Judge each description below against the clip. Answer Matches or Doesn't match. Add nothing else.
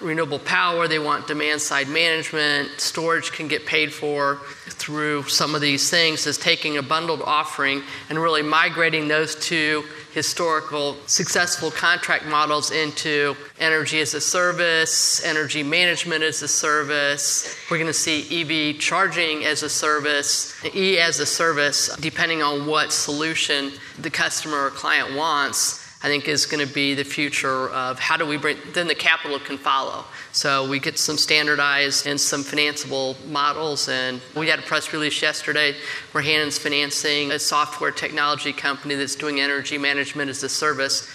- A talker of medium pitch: Matches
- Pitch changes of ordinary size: Doesn't match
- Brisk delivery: Doesn't match